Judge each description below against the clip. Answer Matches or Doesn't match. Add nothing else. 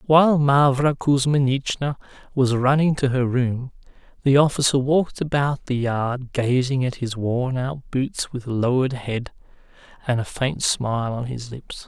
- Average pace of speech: Matches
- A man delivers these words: Matches